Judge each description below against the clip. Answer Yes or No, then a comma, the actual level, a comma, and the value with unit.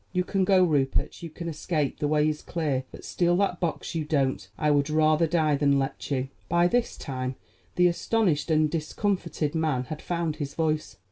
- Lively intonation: No, average, 3.1 semitones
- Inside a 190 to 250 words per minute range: Yes, average, 195 wpm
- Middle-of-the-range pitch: Yes, medium, 155 Hz